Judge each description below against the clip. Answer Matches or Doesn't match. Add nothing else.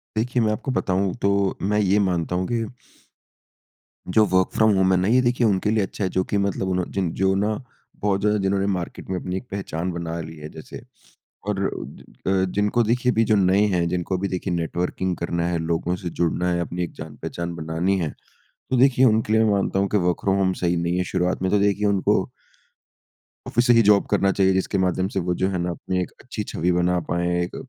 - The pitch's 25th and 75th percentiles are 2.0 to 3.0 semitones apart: Matches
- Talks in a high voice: Doesn't match